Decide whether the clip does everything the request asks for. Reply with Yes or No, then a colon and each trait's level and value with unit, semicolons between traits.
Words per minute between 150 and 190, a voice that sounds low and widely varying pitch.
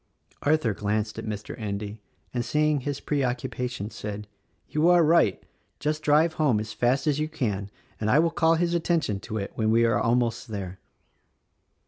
Yes: average, 175 wpm; low, 120 Hz; wide, 6.3 semitones